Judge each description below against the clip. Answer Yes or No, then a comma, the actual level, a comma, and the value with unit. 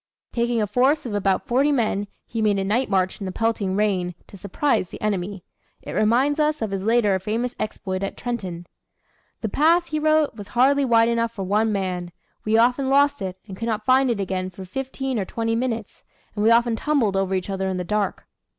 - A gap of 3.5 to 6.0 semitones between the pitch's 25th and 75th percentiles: Yes, average, 4.3 semitones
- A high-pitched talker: Yes, high, 220 Hz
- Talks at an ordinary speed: No, fast, 215 wpm